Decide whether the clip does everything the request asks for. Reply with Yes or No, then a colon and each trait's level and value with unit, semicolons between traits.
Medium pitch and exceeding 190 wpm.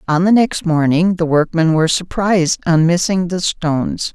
No: medium, 170 Hz; average, 175 wpm